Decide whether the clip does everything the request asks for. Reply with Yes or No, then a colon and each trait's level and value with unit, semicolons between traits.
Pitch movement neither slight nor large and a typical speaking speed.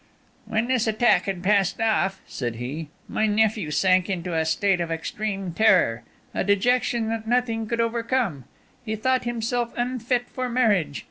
Yes: average, 4.4 semitones; average, 155 wpm